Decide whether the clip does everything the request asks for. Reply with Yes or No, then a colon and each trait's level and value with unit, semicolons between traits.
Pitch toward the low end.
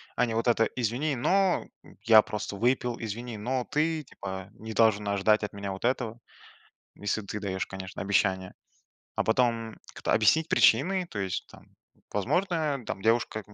Yes: low, 115 Hz